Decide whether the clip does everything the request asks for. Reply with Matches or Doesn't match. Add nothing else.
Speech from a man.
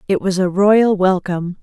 Doesn't match